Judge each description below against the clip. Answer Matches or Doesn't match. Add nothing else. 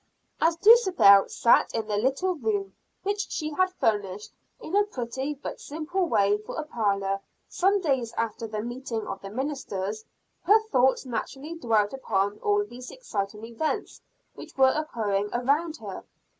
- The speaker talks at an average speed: Matches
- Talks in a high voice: Matches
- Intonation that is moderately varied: Doesn't match